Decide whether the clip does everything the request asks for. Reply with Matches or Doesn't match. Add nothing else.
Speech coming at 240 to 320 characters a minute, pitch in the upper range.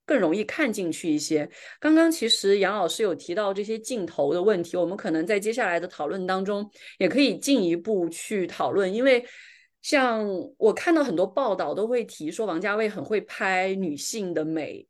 Matches